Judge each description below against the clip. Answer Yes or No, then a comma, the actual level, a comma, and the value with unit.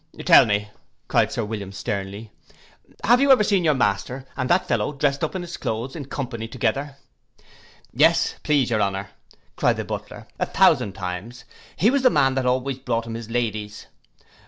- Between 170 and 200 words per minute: Yes, average, 180 wpm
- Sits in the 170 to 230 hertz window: No, low, 120 Hz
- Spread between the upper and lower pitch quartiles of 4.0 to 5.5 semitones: Yes, average, 5.2 semitones